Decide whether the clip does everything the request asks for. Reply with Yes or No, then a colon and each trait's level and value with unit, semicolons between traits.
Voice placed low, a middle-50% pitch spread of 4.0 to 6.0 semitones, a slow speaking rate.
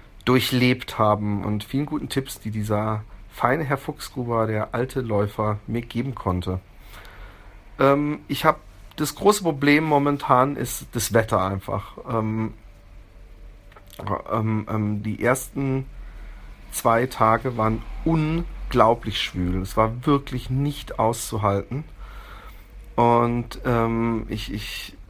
Yes: low, 110 Hz; average, 4.4 semitones; slow, 110 wpm